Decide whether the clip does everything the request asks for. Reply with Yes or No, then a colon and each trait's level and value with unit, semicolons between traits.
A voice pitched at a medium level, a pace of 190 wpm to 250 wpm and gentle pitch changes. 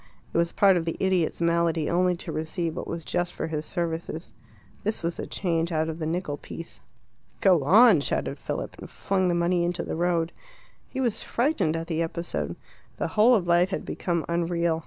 Yes: medium, 170 Hz; average, 200 wpm; narrow, 1.8 semitones